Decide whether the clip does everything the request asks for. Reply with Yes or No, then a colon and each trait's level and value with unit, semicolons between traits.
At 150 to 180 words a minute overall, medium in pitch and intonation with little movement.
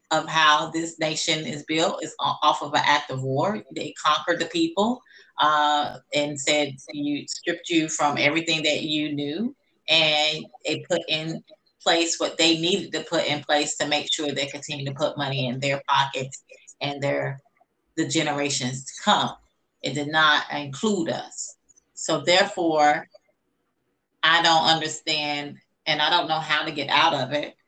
Yes: average, 165 wpm; medium, 155 Hz; narrow, 2.0 semitones